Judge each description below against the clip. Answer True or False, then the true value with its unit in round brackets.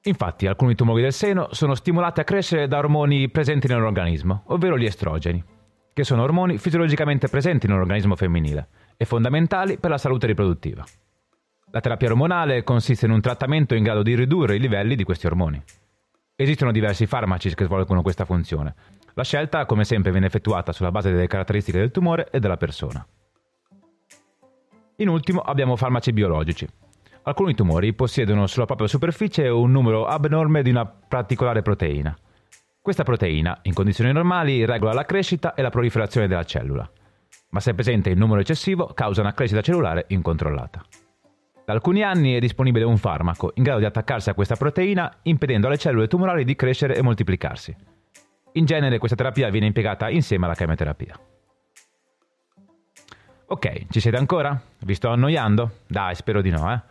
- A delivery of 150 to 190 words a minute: True (160 wpm)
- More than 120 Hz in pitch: False (115 Hz)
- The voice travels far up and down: True (6.5 semitones)